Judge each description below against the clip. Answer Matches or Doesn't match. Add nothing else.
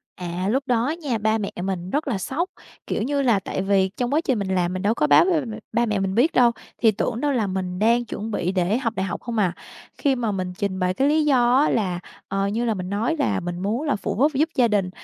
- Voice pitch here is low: Doesn't match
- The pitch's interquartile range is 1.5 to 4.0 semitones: Doesn't match